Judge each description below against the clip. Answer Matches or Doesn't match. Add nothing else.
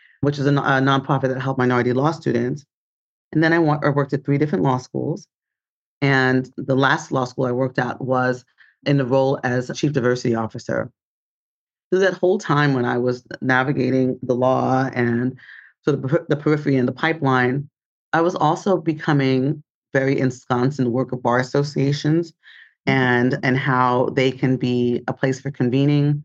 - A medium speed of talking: Matches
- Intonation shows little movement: Matches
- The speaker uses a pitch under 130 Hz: Doesn't match